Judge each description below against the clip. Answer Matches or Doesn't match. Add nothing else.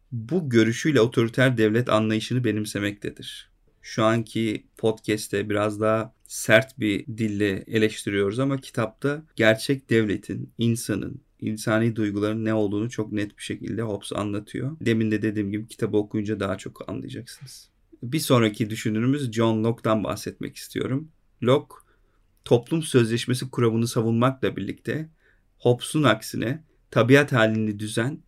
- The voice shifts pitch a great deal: Doesn't match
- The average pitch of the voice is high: Doesn't match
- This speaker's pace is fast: Doesn't match